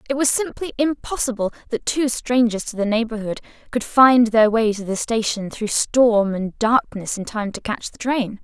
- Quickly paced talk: No, average, 190 wpm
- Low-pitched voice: No, high, 230 Hz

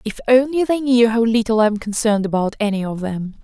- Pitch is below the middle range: No, high, 225 Hz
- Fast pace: Yes, fast, 225 wpm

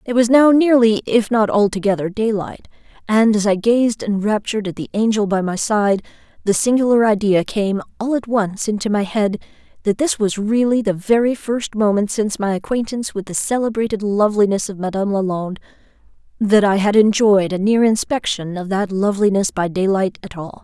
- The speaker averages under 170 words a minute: No, average, 175 wpm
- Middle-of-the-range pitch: No, high, 210 Hz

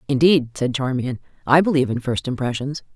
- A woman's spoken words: Yes, female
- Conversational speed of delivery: Yes, average, 165 wpm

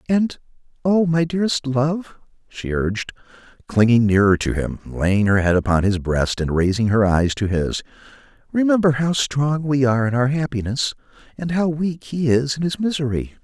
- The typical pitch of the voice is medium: No, low, 130 Hz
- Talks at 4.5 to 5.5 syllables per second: Yes, 5.0 syllables/s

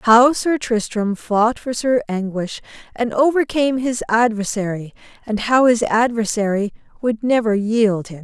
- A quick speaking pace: No, average, 140 wpm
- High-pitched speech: Yes, high, 225 Hz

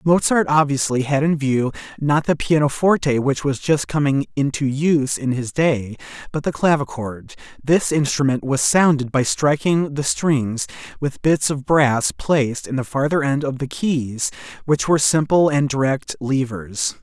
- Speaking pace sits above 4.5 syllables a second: No, 4.4 syllables/s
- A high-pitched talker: No, medium, 140 Hz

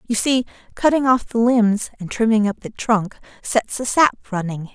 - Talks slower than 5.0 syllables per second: Yes, 4.7 syllables/s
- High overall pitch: Yes, high, 225 Hz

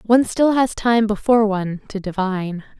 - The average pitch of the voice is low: No, high, 215 Hz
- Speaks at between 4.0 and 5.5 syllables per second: Yes, 5.4 syllables/s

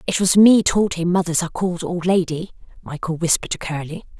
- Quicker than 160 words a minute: Yes, average, 200 wpm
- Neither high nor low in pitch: Yes, medium, 175 Hz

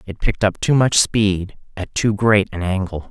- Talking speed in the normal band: No, fast, 210 wpm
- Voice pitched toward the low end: Yes, low, 100 Hz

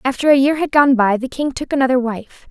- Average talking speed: No, fast, 265 wpm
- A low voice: No, very high, 265 Hz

